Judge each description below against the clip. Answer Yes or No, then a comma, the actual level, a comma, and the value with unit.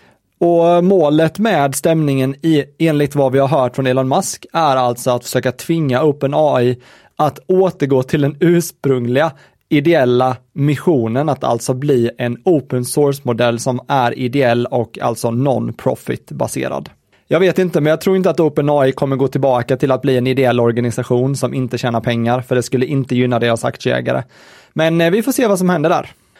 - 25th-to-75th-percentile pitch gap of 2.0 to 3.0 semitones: No, average, 4.0 semitones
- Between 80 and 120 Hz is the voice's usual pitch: No, low, 135 Hz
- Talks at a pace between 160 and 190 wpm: Yes, average, 170 wpm